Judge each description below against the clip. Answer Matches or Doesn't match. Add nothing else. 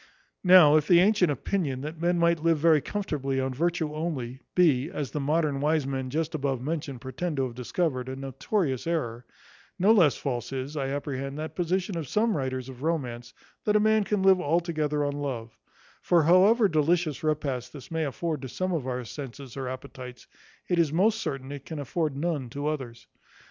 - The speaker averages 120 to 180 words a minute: Doesn't match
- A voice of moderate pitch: Matches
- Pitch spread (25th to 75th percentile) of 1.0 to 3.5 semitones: Doesn't match